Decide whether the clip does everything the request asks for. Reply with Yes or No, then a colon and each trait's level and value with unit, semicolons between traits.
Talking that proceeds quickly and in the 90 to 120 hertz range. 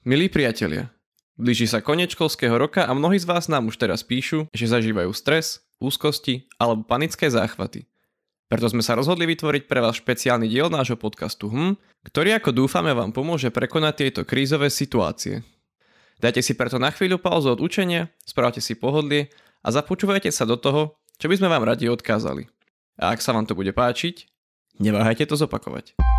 No: fast, 170 wpm; low, 135 Hz